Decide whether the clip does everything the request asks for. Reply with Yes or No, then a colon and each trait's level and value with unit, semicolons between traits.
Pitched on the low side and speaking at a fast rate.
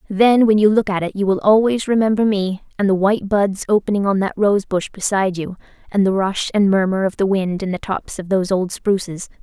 No: high, 200 Hz; fast, 230 wpm